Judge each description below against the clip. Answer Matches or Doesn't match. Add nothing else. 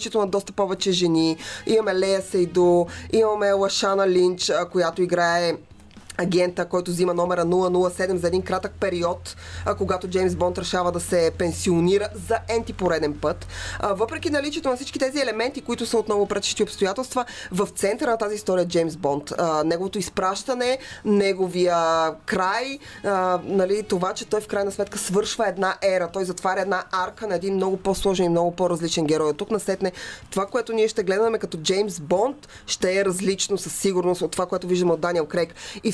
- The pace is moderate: Doesn't match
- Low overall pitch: Doesn't match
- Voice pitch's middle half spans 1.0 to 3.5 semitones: Matches